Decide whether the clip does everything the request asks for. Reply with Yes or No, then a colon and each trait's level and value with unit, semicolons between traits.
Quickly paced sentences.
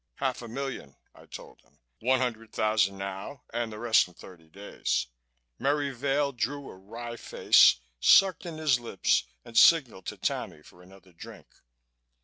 No: average, 160 wpm